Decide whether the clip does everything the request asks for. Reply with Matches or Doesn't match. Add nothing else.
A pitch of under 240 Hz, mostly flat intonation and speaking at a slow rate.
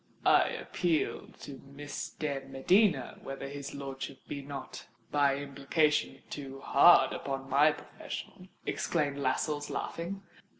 Matches